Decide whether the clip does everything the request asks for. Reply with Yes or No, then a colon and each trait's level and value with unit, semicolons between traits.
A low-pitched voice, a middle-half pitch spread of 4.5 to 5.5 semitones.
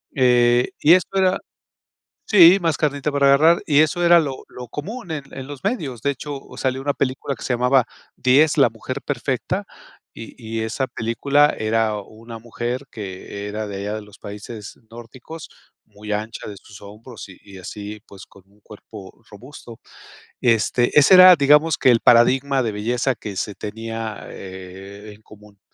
Yes: low, 120 Hz; average, 5.0 semitones